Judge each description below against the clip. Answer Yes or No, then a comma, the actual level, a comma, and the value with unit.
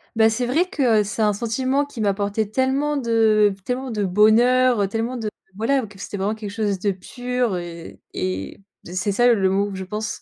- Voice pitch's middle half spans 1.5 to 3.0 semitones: No, average, 3.7 semitones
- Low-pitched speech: No, high, 220 Hz